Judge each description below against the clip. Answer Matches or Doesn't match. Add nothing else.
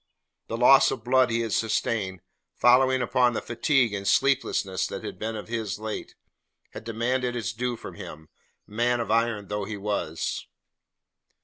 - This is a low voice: Matches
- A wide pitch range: Doesn't match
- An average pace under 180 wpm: Matches